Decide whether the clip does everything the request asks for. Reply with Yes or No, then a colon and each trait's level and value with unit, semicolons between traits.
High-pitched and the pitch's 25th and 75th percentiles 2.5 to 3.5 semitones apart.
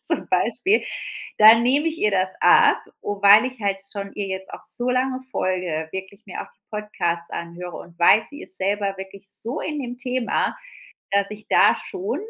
No: high, 205 Hz; average, 4.7 semitones